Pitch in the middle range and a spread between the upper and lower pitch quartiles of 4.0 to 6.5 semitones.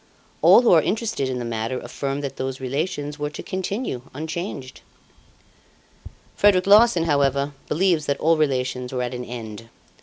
Yes: medium, 145 Hz; average, 5.1 semitones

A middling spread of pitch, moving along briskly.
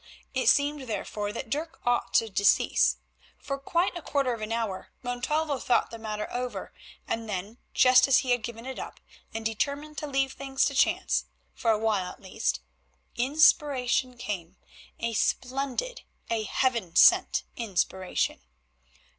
No: average, 3.9 semitones; average, 155 wpm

